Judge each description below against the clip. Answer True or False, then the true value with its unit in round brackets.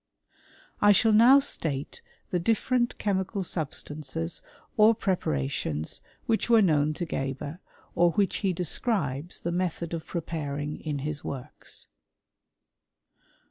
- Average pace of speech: False (115 wpm)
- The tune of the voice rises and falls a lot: True (5.9 semitones)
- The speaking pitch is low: False (170 Hz)